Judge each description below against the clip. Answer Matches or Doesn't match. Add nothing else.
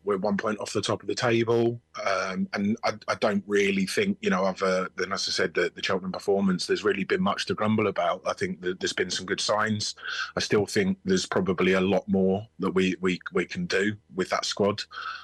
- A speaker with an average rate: Doesn't match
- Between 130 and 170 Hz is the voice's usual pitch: Doesn't match